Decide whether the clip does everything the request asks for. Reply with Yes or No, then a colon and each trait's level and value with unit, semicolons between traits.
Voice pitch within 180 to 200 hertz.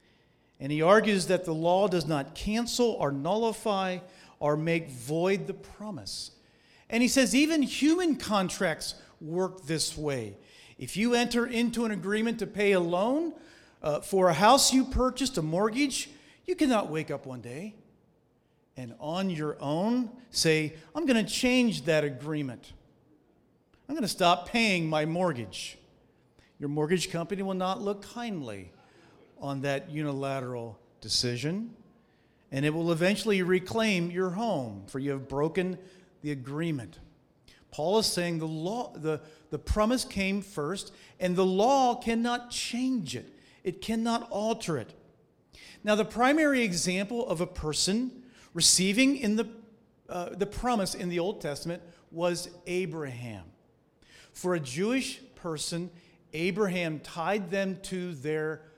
Yes: medium, 185 Hz